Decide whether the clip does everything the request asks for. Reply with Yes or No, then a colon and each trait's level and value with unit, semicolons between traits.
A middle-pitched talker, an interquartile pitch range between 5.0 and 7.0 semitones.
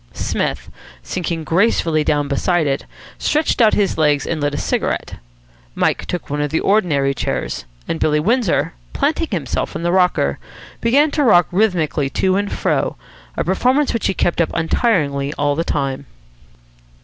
Yes: medium, 170 Hz; wide, 5.6 semitones